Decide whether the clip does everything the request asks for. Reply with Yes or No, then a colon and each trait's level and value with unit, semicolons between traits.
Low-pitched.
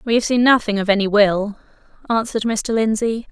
No: high, 220 Hz